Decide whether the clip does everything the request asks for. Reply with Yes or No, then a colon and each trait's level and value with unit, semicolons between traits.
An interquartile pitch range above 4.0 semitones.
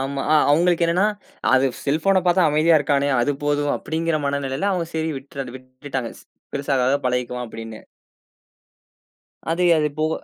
No: average, 3.7 semitones